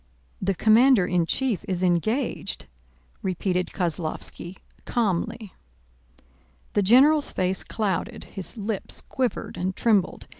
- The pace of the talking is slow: Yes, slow, 105 wpm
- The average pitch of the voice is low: No, high, 195 Hz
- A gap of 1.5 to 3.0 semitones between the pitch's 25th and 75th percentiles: No, average, 4.1 semitones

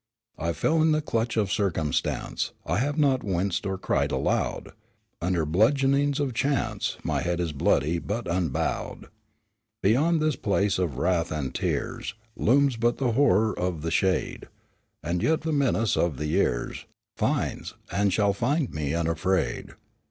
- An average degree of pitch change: No, wide, 8.0 semitones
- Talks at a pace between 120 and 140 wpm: No, average, 150 wpm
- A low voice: Yes, low, 100 Hz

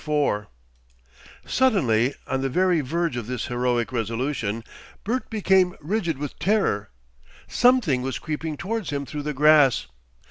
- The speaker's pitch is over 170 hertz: No, medium, 145 Hz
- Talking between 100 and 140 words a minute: Yes, slow, 135 wpm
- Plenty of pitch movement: Yes, wide, 6.5 semitones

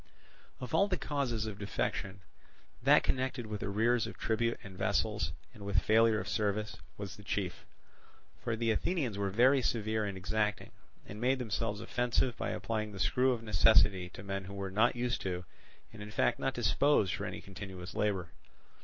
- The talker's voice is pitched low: Yes, low, 110 Hz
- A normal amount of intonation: Yes, average, 3.1 semitones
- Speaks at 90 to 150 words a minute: No, average, 180 wpm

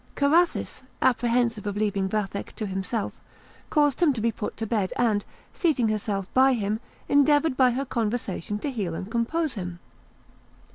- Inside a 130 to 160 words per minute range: Yes, average, 155 wpm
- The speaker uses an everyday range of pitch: Yes, average, 4.5 semitones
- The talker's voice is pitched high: Yes, high, 230 Hz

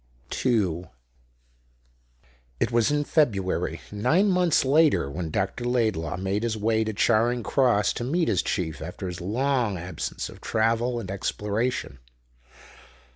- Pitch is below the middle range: Yes, low, 110 Hz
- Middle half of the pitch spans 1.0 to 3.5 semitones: No, average, 4.8 semitones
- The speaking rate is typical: No, slow, 130 wpm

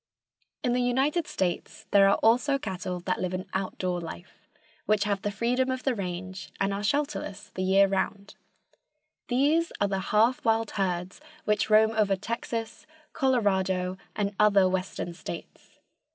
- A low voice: No, high, 200 Hz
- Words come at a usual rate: Yes, average, 150 wpm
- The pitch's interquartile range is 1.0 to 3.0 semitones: No, average, 3.7 semitones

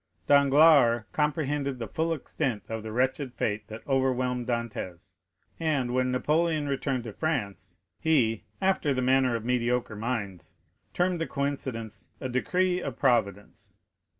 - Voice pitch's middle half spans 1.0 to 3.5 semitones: No, average, 3.9 semitones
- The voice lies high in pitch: No, low, 130 Hz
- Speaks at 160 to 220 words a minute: No, slow, 135 wpm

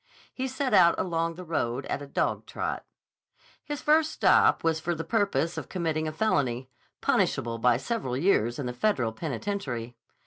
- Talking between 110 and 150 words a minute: No, average, 165 wpm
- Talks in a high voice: No, medium, 160 Hz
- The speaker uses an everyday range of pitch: No, wide, 8.1 semitones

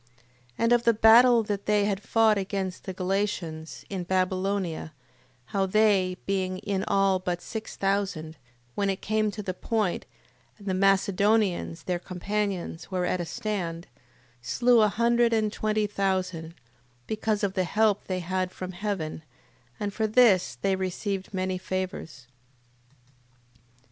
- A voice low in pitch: No, high, 195 Hz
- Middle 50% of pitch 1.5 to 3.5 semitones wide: Yes, narrow, 2.4 semitones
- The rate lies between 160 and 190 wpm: No, average, 145 wpm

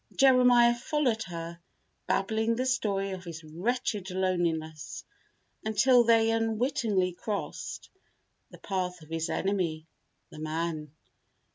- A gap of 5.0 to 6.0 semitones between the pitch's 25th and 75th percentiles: Yes, wide, 5.6 semitones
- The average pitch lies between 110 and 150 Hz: No, high, 195 Hz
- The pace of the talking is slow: Yes, slow, 110 wpm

